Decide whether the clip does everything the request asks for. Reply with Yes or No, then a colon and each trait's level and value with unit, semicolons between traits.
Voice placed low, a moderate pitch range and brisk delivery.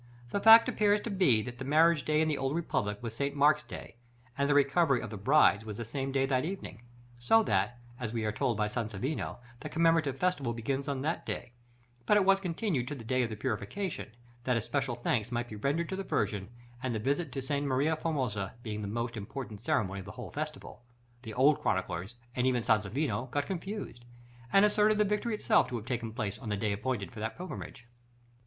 No: low, 130 Hz; wide, 5.8 semitones; fast, 215 wpm